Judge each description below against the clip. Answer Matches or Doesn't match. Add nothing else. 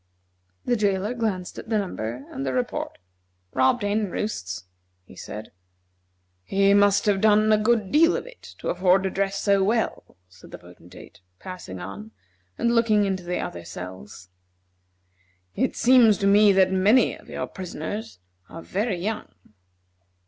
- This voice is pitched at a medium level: Doesn't match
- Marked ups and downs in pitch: Matches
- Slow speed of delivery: Doesn't match